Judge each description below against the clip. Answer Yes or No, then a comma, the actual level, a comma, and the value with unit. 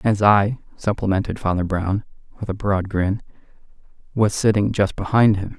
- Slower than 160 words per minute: Yes, average, 150 wpm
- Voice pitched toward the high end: No, low, 100 Hz